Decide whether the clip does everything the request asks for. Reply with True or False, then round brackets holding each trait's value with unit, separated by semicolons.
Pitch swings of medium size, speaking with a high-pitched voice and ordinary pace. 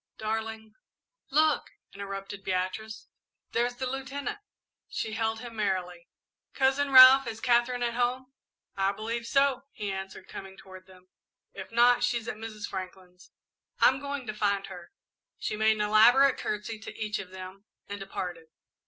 True (4.0 semitones; 220 Hz; 155 wpm)